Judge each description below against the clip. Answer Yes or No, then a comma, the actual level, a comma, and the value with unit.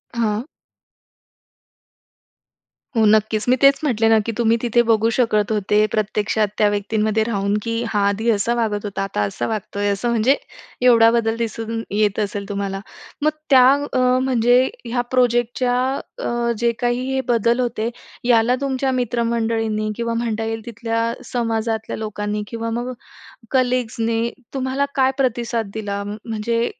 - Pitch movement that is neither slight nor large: No, narrow, 2.0 semitones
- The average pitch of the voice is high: Yes, high, 225 Hz